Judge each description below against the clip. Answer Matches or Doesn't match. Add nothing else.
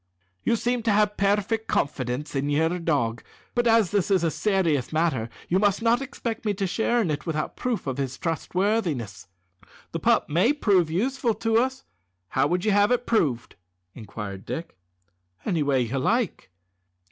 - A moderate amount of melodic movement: Doesn't match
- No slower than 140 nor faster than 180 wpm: Matches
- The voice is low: Doesn't match